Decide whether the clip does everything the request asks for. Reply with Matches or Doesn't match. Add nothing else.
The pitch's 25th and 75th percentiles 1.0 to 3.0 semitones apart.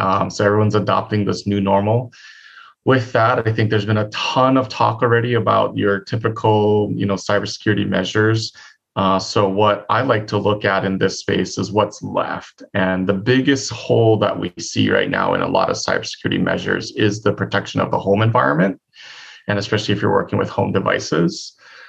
Matches